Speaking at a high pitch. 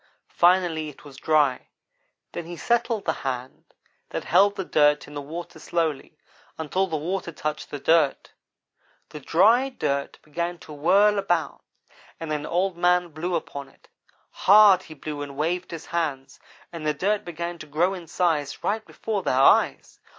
No: medium, 165 Hz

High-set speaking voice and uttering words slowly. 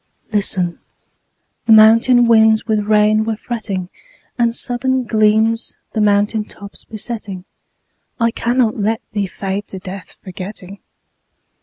Yes: high, 215 Hz; slow, 120 wpm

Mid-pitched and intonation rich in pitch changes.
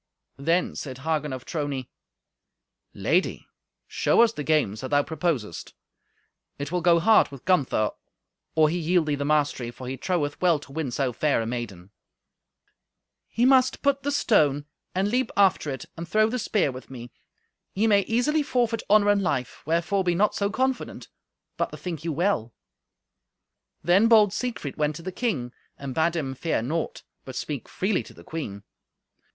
Yes: medium, 160 Hz; wide, 6.7 semitones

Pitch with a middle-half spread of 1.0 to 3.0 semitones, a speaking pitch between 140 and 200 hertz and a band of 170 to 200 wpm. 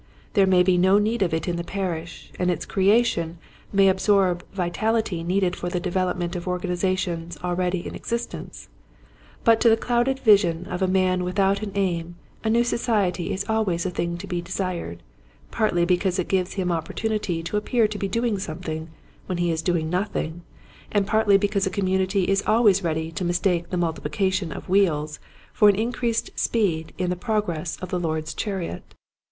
Yes: average, 2.7 semitones; medium, 185 Hz; average, 185 wpm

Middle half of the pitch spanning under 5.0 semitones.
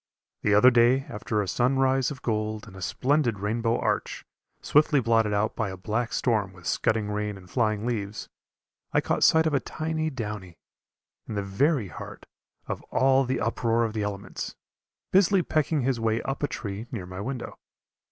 Yes: average, 4.3 semitones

